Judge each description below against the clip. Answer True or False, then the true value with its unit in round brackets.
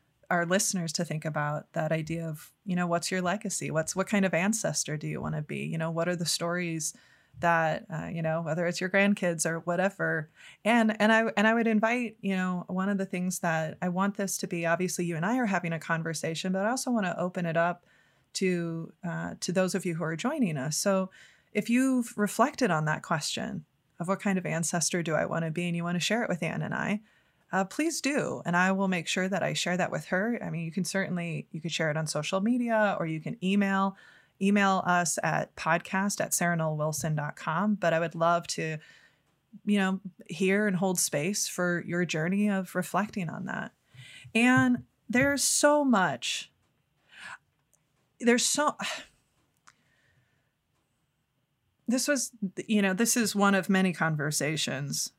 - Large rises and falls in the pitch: False (3.8 semitones)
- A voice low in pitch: False (180 Hz)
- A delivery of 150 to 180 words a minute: False (195 wpm)